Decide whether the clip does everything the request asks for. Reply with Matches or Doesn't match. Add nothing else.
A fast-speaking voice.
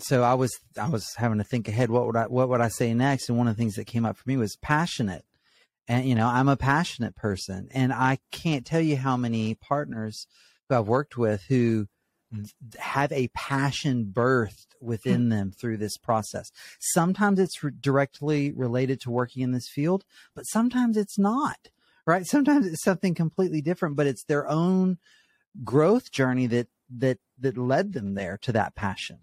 Doesn't match